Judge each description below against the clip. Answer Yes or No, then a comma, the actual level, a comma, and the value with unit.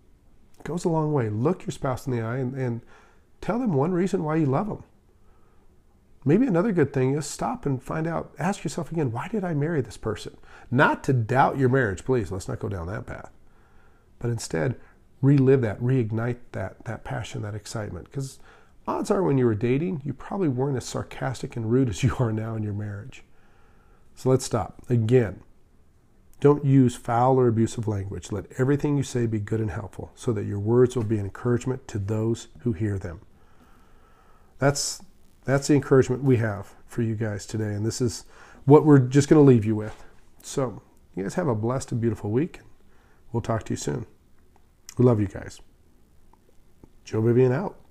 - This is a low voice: Yes, low, 120 Hz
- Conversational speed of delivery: Yes, average, 195 wpm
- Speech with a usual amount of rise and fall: Yes, average, 4.1 semitones